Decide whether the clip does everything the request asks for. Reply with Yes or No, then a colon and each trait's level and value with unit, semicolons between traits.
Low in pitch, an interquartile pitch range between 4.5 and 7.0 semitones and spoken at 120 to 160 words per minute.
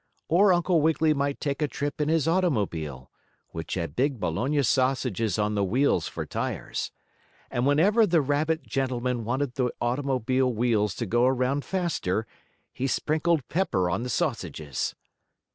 Yes: low, 130 Hz; average, 5.1 semitones; average, 150 wpm